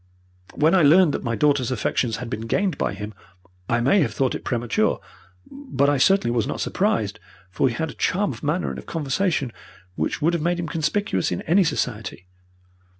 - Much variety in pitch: Yes, wide, 6.6 semitones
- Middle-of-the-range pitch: Yes, medium, 145 Hz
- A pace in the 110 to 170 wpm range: No, average, 200 wpm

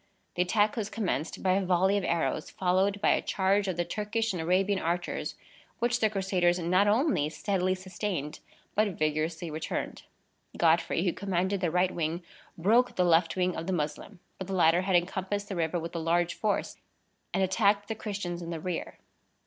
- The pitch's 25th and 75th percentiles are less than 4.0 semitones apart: Yes, average, 2.8 semitones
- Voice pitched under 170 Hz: No, medium, 185 Hz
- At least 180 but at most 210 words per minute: Yes, average, 185 wpm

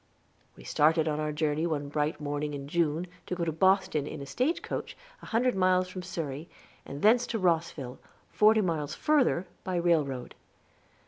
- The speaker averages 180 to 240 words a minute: No, average, 170 wpm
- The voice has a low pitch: No, medium, 160 Hz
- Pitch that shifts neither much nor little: Yes, average, 3.9 semitones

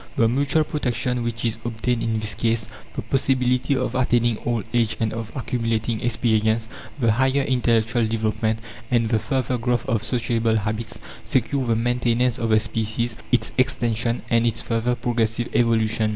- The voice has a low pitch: Yes, low, 115 Hz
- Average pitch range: No, narrow, 1.7 semitones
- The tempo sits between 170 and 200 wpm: No, average, 160 wpm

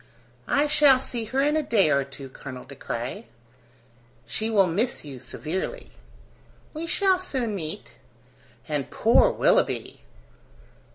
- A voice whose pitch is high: Yes, high, 220 Hz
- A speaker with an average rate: No, slow, 130 wpm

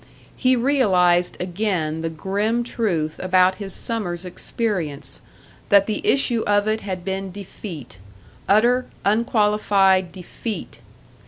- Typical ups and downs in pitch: Yes, average, 3.5 semitones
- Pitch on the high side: Yes, high, 195 Hz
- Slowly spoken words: Yes, slow, 110 wpm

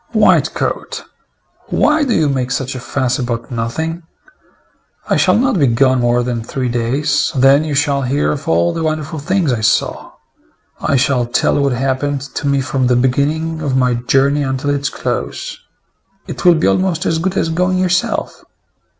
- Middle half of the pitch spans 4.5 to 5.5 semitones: No, average, 4.1 semitones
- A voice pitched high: No, medium, 140 Hz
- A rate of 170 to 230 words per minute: Yes, average, 175 wpm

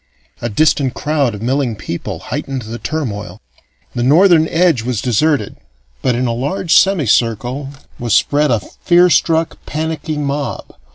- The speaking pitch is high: No, medium, 140 Hz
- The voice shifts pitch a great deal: No, average, 5.0 semitones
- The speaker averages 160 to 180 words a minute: No, average, 140 wpm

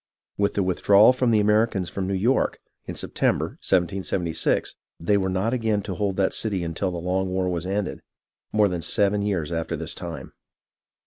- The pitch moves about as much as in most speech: No, narrow, 2.2 semitones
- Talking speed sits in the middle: Yes, average, 180 wpm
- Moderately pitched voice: No, very low, 95 Hz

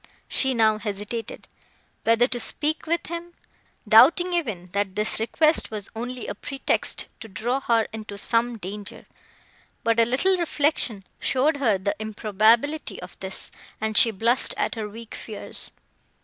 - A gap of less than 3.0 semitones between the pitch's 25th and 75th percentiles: No, average, 4.2 semitones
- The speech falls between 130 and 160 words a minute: Yes, average, 150 wpm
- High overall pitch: Yes, high, 230 Hz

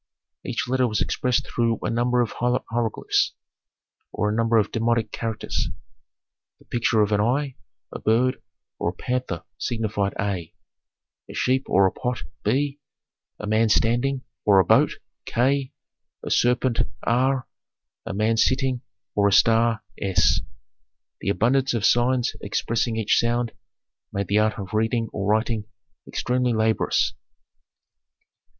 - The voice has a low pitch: Yes, low, 115 Hz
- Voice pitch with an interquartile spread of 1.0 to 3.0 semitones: Yes, average, 2.7 semitones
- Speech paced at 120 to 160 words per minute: Yes, average, 140 wpm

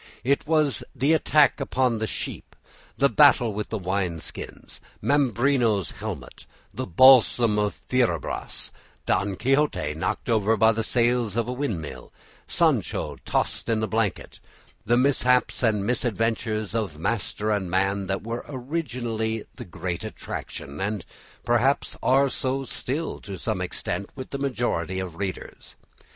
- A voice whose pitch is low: Yes, low, 115 Hz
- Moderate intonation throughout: Yes, average, 4.4 semitones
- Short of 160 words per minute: Yes, average, 140 wpm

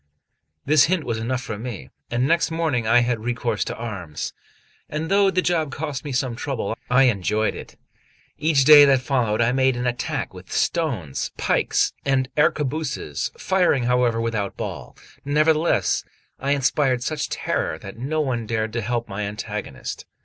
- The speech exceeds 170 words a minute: No, average, 165 wpm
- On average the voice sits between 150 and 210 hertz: No, low, 125 Hz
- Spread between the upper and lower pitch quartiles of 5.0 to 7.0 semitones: No, average, 4.4 semitones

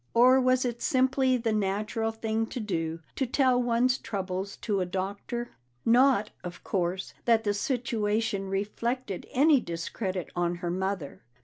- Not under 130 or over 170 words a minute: Yes, average, 150 wpm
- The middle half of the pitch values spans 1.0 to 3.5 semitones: No, average, 4.5 semitones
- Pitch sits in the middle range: No, high, 220 Hz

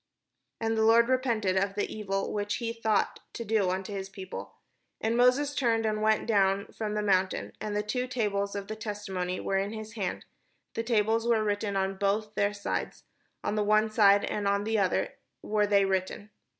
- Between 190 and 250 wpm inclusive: Yes, average, 200 wpm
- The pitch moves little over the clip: Yes, narrow, 2.0 semitones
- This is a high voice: Yes, high, 210 Hz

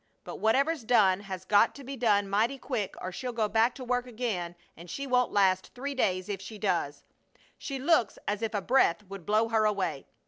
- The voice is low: No, high, 215 Hz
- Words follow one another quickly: Yes, fast, 210 wpm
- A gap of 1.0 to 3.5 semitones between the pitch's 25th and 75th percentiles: No, average, 4.2 semitones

